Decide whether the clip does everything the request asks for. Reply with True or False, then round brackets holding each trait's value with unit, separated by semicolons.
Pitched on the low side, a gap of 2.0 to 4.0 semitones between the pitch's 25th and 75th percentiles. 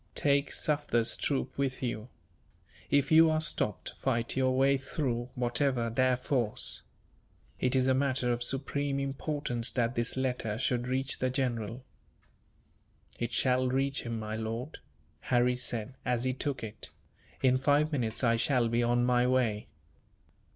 True (125 Hz; 2.4 semitones)